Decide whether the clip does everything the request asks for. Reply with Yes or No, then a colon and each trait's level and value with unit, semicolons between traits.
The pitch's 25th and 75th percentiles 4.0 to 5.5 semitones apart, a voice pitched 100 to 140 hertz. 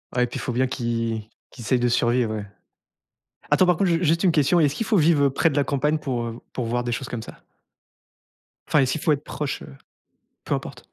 Yes: average, 4.4 semitones; low, 135 Hz